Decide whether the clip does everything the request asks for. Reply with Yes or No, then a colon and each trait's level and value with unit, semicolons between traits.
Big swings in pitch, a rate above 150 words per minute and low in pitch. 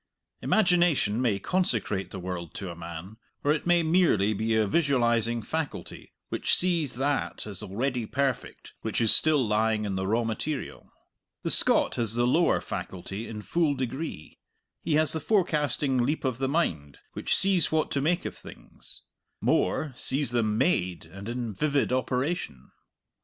Yes: wide, 6.3 semitones; average, 160 wpm; low, 125 Hz